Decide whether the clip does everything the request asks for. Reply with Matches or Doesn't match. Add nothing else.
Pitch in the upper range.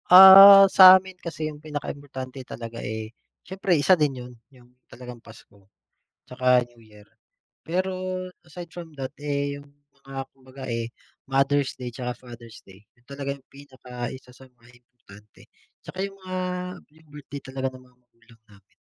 Doesn't match